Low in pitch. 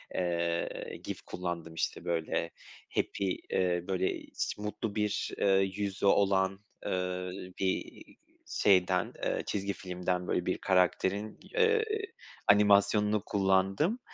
Yes: very low, 95 Hz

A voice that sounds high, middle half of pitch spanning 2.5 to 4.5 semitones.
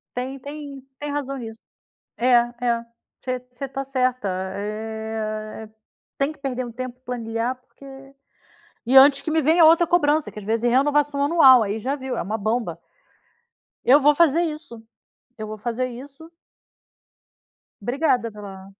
Yes: very high, 255 Hz; average, 4.2 semitones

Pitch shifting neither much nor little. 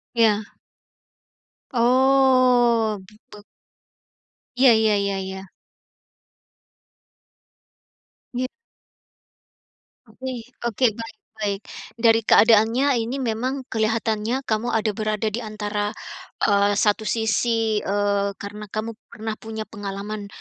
No: narrow, 2.2 semitones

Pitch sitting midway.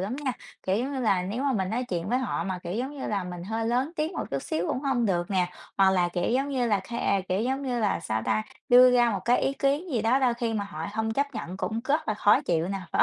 No: high, 225 Hz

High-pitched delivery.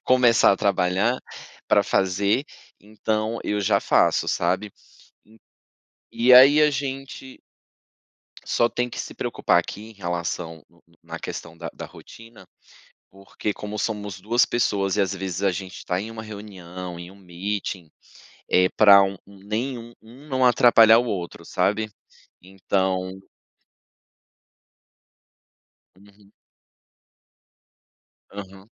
No: low, 100 Hz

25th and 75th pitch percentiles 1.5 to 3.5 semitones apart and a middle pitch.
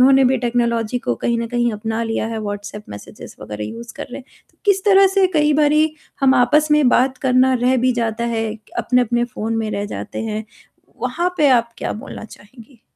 No: average, 3.2 semitones; high, 240 Hz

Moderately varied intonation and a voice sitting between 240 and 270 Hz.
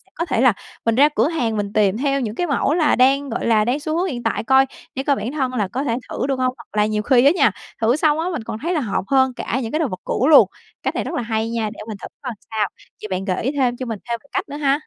Yes: average, 4.1 semitones; very high, 255 Hz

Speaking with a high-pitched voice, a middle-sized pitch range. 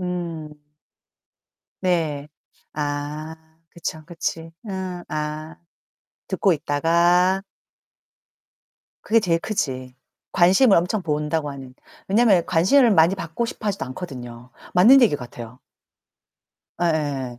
No: medium, 165 Hz; average, 4.0 semitones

